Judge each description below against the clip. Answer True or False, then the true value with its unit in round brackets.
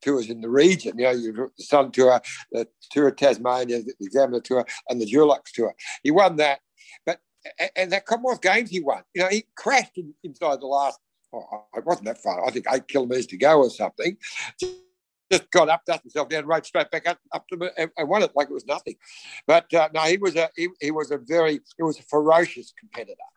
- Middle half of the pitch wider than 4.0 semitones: True (5.0 semitones)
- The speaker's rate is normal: False (235 wpm)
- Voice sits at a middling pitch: True (160 Hz)